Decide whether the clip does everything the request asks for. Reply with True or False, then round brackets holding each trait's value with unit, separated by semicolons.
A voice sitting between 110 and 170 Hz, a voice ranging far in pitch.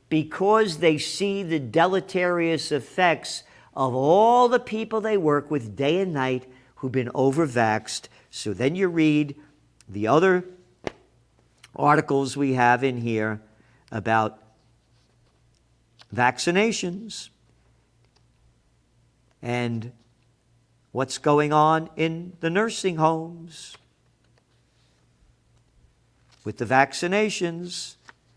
True (140 Hz; 6.2 semitones)